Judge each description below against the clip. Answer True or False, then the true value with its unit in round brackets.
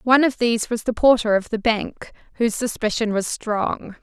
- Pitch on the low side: False (230 Hz)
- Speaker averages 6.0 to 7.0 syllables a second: False (5.2 syllables/s)